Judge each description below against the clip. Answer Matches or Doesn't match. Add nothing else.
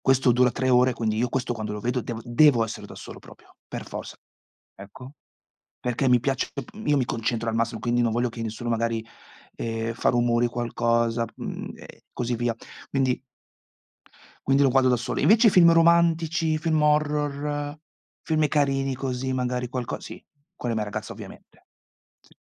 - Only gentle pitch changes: Doesn't match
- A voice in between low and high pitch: Doesn't match